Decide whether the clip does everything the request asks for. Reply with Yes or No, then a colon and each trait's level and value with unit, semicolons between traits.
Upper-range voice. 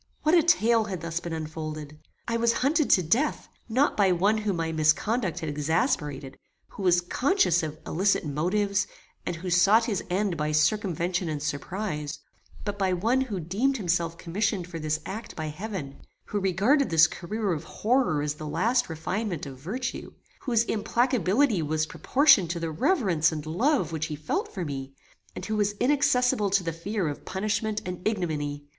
No: medium, 180 Hz